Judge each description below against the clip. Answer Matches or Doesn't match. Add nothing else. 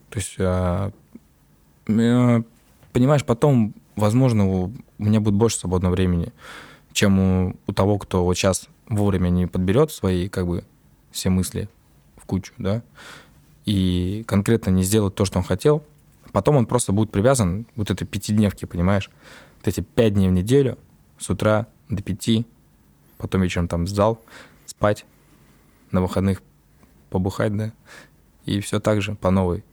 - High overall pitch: Doesn't match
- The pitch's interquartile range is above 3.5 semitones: Doesn't match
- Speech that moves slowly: Doesn't match